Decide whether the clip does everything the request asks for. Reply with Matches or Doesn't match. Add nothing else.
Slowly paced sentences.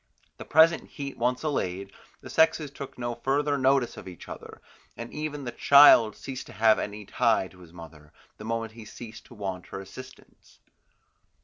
Doesn't match